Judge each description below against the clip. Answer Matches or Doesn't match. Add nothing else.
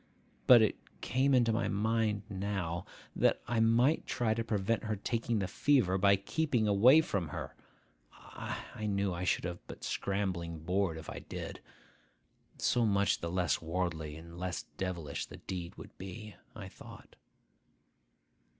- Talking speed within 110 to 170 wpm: Matches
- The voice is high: Doesn't match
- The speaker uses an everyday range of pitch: Matches